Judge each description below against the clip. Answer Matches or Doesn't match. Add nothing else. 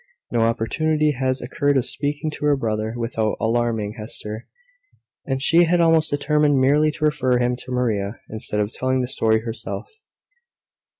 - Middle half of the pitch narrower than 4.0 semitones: Doesn't match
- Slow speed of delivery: Doesn't match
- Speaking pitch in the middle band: Doesn't match